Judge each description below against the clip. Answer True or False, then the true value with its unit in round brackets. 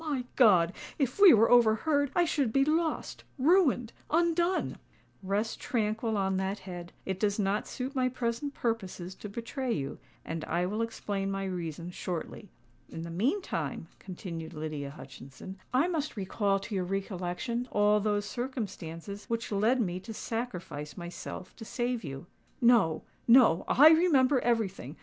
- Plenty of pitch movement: True (5.7 semitones)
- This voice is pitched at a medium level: False (210 Hz)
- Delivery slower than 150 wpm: True (140 wpm)